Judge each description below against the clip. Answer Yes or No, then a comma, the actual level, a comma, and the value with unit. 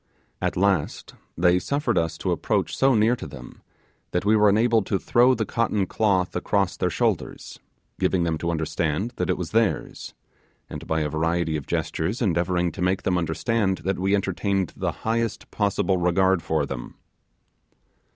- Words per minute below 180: Yes, average, 170 wpm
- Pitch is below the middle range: Yes, very low, 95 Hz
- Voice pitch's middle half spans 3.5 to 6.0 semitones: Yes, average, 4.0 semitones